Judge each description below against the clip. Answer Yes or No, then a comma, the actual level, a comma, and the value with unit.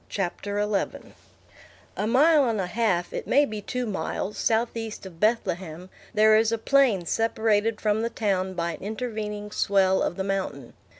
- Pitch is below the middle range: No, high, 210 Hz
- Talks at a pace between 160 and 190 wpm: Yes, average, 165 wpm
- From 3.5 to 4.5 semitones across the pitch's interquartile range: No, average, 3.0 semitones